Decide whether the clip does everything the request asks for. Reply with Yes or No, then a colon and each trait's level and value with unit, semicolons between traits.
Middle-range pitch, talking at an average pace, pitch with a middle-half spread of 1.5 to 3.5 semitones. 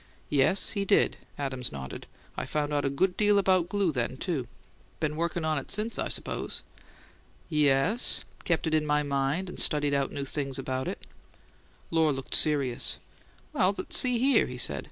No: medium, 150 Hz; average, 175 wpm; average, 5.1 semitones